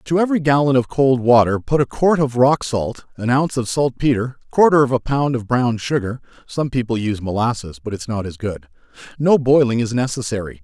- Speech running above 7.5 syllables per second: Yes, 7.8 syllables/s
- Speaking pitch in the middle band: No, low, 125 Hz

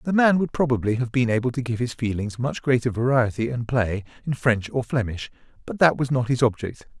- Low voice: Yes, low, 125 Hz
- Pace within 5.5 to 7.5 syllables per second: Yes, 5.6 syllables/s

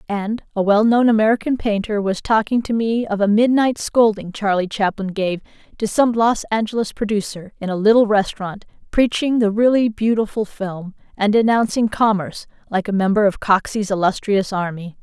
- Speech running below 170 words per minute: Yes, average, 160 wpm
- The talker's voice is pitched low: No, high, 210 Hz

